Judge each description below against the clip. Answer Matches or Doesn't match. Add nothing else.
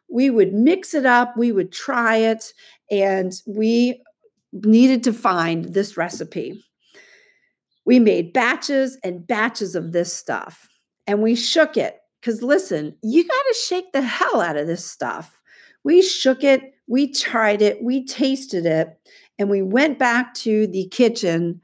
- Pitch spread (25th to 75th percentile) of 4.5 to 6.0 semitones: Matches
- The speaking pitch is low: Doesn't match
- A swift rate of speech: Doesn't match